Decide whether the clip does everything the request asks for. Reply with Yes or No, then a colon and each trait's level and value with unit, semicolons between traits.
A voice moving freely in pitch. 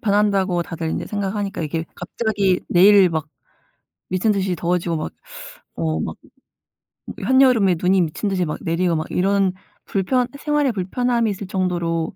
No: average, 3.2 semitones